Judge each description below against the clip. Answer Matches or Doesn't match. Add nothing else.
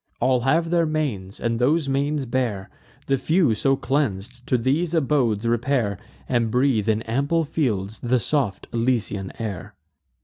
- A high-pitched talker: Doesn't match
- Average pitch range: Matches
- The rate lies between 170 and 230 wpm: Doesn't match